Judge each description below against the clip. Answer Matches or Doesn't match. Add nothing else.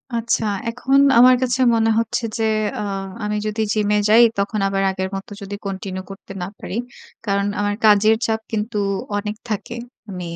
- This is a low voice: Doesn't match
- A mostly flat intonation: Matches